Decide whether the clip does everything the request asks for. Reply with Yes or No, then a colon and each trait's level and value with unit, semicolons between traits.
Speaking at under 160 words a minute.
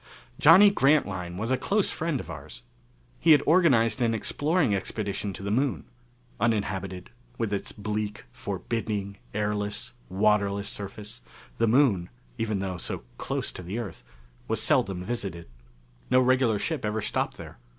Yes: average, 145 wpm